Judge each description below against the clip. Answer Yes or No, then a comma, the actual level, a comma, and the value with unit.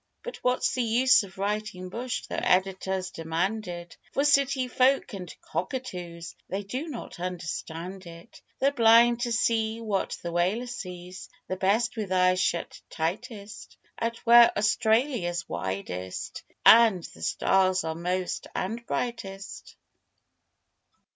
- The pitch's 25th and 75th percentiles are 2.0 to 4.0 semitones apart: No, average, 4.7 semitones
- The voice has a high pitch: Yes, high, 195 Hz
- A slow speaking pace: Yes, slow, 130 wpm